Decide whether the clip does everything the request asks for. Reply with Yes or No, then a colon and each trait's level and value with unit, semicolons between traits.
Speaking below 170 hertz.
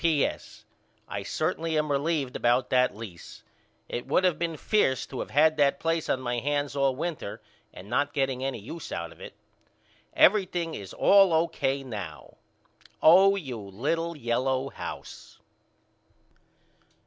Yes: medium, 140 Hz